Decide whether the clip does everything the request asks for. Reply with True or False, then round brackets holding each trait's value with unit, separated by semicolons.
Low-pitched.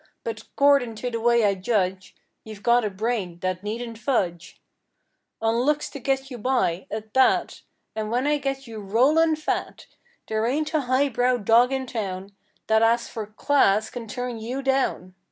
False (235 Hz)